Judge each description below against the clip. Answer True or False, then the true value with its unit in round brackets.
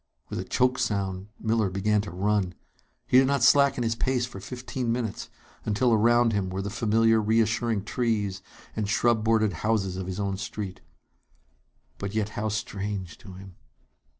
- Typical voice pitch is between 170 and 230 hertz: False (110 Hz)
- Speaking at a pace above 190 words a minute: False (165 wpm)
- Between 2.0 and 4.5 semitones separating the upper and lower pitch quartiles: True (2.9 semitones)